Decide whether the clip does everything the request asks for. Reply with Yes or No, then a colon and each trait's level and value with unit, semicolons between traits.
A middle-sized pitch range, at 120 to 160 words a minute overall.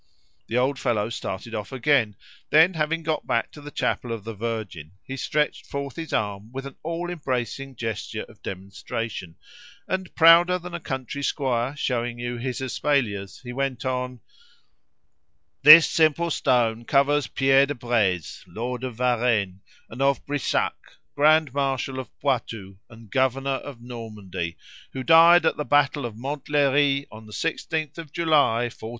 Yes: average, 4.2 semitones; average, 155 wpm